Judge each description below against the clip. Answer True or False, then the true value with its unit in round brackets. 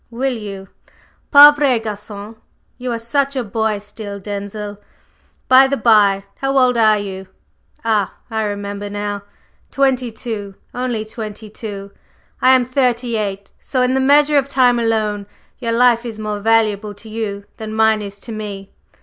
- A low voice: False (220 Hz)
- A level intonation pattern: False (3.3 semitones)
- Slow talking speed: False (160 wpm)